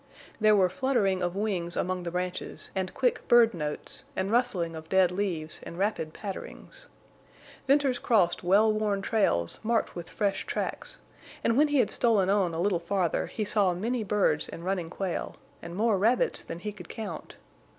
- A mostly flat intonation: No, average, 3.8 semitones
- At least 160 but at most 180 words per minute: Yes, average, 175 wpm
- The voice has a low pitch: No, high, 195 Hz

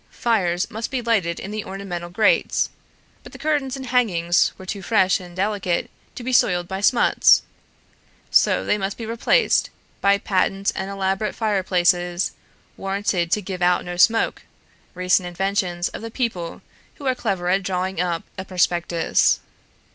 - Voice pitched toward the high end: Yes, high, 195 Hz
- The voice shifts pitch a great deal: No, average, 3.4 semitones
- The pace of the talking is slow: No, average, 155 wpm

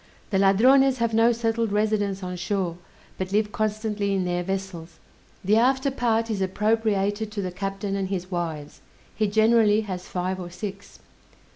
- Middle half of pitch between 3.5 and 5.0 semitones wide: No, average, 2.9 semitones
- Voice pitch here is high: Yes, high, 205 Hz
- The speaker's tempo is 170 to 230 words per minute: No, average, 160 wpm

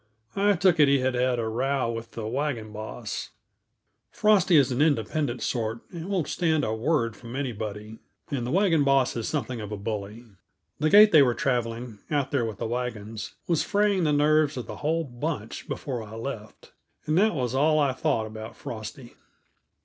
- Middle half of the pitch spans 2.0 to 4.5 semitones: No, average, 5.2 semitones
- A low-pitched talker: Yes, low, 130 Hz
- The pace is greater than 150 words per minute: Yes, average, 190 wpm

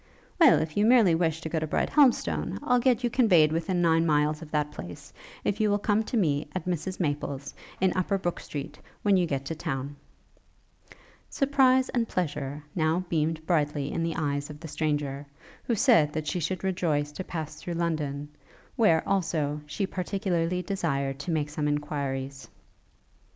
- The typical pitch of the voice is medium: Yes, medium, 160 Hz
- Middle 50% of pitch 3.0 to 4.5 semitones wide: Yes, average, 4.2 semitones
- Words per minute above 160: Yes, average, 175 wpm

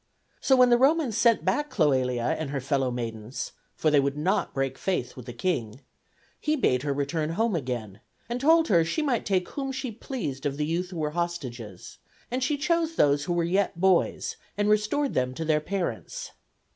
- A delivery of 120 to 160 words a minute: No, average, 195 wpm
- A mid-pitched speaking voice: Yes, medium, 170 Hz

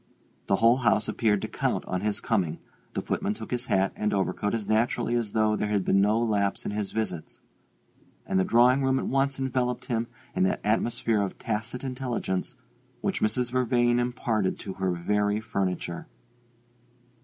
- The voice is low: Yes, low, 110 Hz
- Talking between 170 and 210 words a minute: Yes, average, 175 wpm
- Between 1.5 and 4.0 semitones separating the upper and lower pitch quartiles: Yes, average, 3.3 semitones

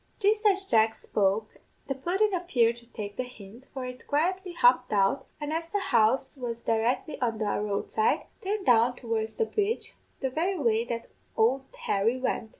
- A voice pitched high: Yes, very high, 250 Hz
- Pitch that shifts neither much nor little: No, wide, 7.4 semitones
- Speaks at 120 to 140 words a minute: No, average, 180 wpm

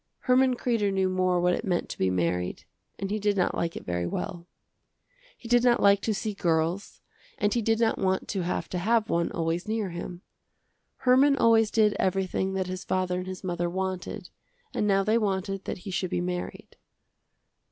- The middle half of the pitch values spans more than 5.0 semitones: No, average, 3.2 semitones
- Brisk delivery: No, average, 195 wpm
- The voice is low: No, high, 190 Hz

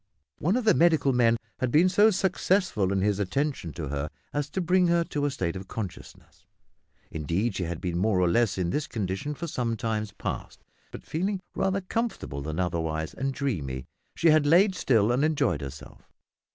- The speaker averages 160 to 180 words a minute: No, average, 190 wpm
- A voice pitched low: Yes, low, 120 Hz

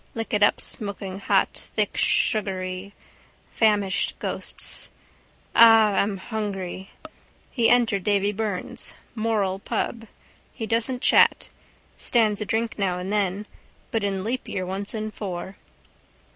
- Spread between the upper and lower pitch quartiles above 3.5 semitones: No, narrow, 2.5 semitones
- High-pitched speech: Yes, high, 205 Hz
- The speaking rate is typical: No, slow, 115 wpm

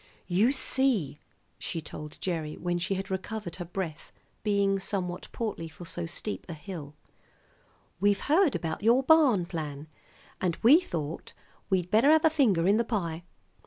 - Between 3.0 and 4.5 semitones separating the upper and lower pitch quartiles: No, average, 5.1 semitones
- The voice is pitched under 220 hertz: Yes, high, 190 Hz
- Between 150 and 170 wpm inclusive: Yes, average, 160 wpm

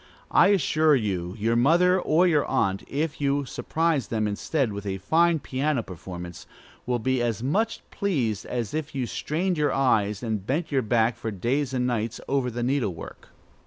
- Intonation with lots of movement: Yes, wide, 5.8 semitones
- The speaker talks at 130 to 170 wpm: No, average, 180 wpm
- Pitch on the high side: No, low, 125 Hz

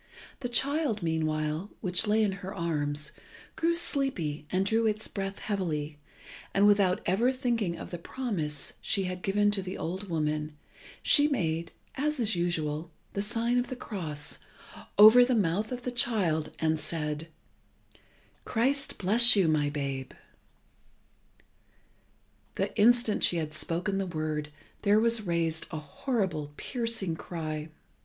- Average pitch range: No, wide, 6.3 semitones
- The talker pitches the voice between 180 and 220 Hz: Yes, high, 190 Hz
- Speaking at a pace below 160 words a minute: Yes, average, 140 wpm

